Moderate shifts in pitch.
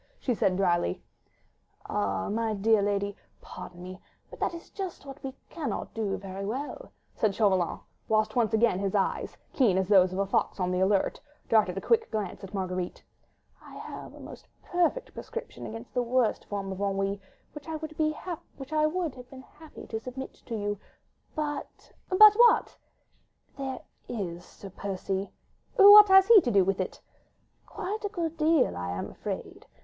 No: wide, 8.0 semitones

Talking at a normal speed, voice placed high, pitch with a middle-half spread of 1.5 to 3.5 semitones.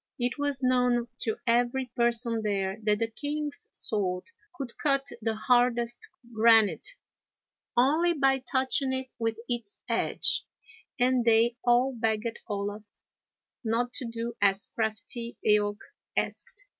No: slow, 125 wpm; high, 235 Hz; narrow, 2.6 semitones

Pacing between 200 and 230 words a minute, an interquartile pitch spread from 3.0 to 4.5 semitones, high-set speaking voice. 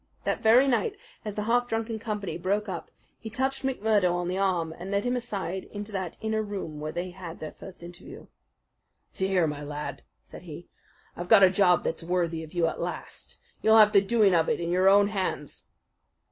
Yes: fast, 205 wpm; average, 3.9 semitones; high, 195 Hz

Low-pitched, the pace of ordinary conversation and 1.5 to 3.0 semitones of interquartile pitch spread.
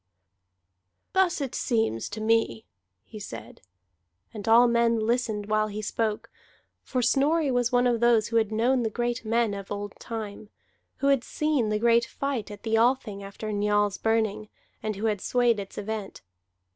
No: high, 225 Hz; average, 170 wpm; narrow, 2.4 semitones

